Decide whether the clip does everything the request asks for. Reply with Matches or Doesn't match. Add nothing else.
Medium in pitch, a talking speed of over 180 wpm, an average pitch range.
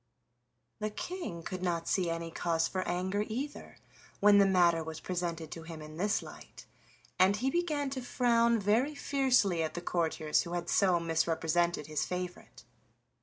Doesn't match